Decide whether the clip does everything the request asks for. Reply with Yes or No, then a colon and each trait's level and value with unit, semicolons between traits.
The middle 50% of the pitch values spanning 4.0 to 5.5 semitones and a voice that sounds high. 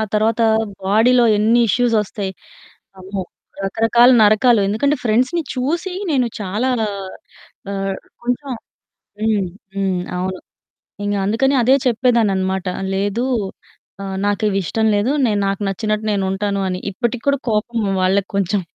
No: average, 3.5 semitones; high, 215 Hz